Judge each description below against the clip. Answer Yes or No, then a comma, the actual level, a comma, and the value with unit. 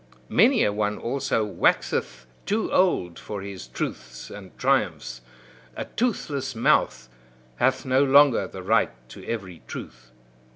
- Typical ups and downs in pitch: No, wide, 6.8 semitones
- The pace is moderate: No, slow, 130 wpm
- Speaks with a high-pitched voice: No, low, 115 Hz